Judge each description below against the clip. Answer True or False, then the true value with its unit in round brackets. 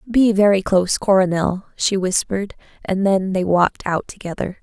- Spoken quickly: False (155 wpm)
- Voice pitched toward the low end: False (190 Hz)